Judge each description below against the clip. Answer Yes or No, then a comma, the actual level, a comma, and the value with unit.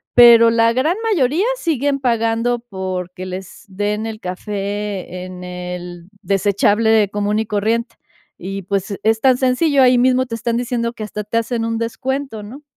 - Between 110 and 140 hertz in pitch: No, high, 225 Hz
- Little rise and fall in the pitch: No, average, 3.6 semitones